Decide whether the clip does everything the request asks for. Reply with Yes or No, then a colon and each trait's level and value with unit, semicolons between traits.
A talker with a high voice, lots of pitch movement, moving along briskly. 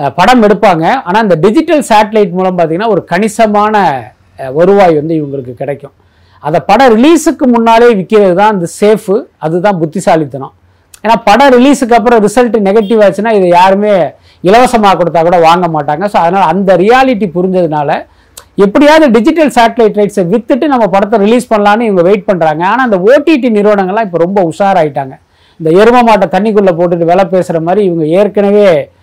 No: high, 205 Hz; average, 4.8 semitones; fast, 150 wpm